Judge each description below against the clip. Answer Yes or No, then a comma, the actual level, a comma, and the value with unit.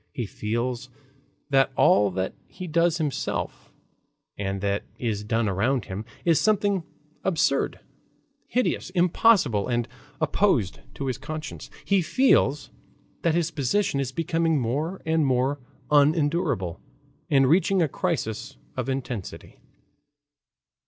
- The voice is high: No, medium, 140 Hz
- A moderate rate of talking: No, slow, 120 wpm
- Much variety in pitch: Yes, wide, 6.2 semitones